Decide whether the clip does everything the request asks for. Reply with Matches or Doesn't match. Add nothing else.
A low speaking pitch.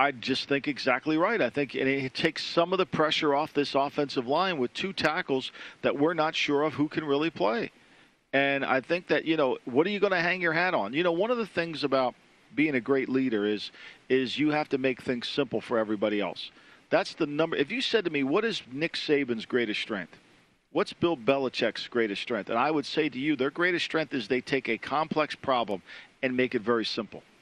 Doesn't match